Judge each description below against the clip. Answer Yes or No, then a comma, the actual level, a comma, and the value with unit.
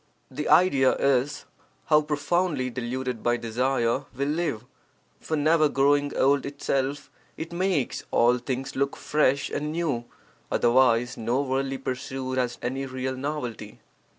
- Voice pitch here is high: No, low, 135 Hz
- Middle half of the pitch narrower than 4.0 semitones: Yes, narrow, 2.4 semitones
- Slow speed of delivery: Yes, slow, 130 wpm